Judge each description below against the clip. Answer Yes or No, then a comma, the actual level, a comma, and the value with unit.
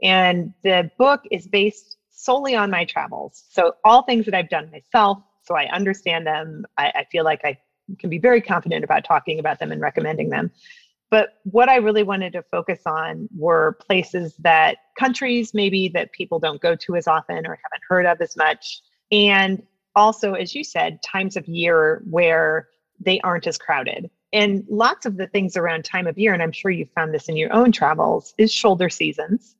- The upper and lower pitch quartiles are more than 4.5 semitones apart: No, average, 4.2 semitones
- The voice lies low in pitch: No, high, 190 Hz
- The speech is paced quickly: No, average, 195 wpm